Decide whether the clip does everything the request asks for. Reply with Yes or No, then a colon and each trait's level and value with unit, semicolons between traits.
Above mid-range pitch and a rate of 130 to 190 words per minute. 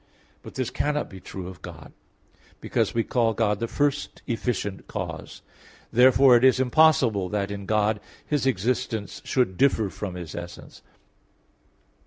No: low, 115 Hz; average, 145 wpm